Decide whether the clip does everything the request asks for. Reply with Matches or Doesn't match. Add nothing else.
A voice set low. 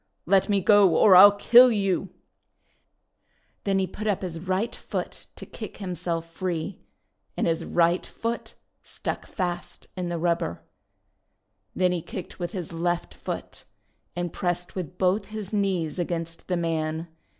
Doesn't match